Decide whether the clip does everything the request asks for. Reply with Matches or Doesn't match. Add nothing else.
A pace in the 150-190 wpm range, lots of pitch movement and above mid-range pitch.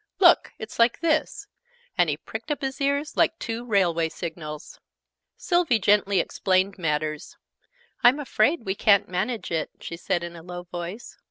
Matches